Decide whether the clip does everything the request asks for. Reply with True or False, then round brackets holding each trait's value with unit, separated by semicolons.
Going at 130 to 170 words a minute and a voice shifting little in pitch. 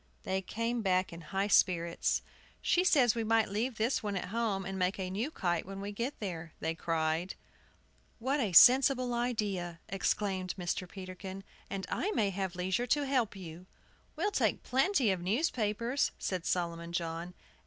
False (165 wpm; 4.6 semitones)